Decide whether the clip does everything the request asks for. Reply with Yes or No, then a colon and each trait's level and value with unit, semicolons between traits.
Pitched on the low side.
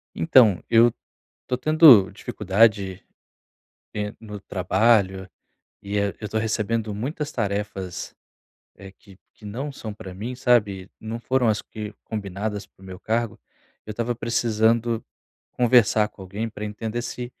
Yes: low, 110 Hz